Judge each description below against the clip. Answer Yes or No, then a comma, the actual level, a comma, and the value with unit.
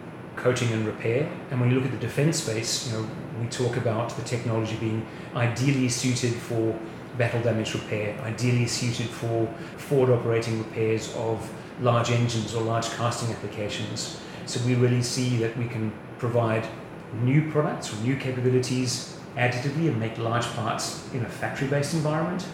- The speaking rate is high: No, average, 160 wpm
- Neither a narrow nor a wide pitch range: No, narrow, 2.3 semitones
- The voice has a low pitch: Yes, low, 120 Hz